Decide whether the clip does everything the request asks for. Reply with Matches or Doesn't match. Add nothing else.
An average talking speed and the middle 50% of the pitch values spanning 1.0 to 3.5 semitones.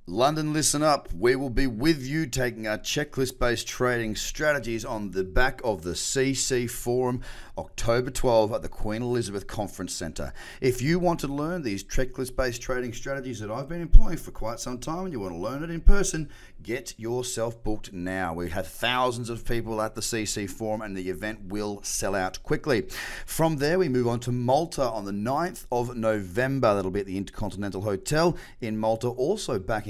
Doesn't match